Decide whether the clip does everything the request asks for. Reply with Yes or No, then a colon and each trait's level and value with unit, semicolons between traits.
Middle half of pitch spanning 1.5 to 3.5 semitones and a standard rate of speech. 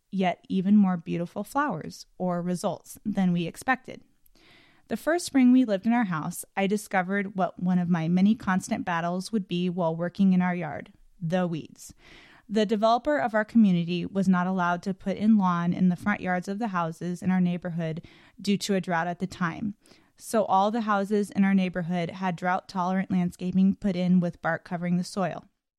Yes: average, 2.8 semitones; average, 195 wpm